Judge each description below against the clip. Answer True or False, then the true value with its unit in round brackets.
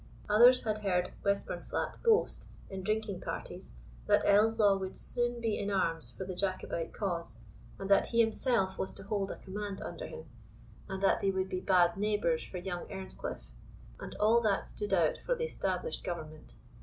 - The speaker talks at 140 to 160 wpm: False (175 wpm)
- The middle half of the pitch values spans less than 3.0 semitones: True (2.5 semitones)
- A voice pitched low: False (195 Hz)